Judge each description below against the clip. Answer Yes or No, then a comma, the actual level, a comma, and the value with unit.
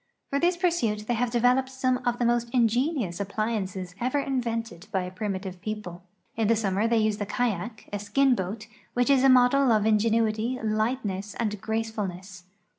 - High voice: Yes, high, 225 Hz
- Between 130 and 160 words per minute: No, average, 175 wpm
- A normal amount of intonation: Yes, average, 3.3 semitones